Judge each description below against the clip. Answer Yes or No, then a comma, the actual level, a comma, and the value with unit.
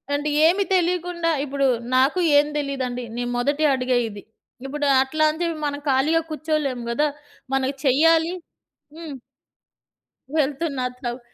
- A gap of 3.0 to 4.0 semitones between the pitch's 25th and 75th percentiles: Yes, average, 3.6 semitones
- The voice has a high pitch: Yes, very high, 285 Hz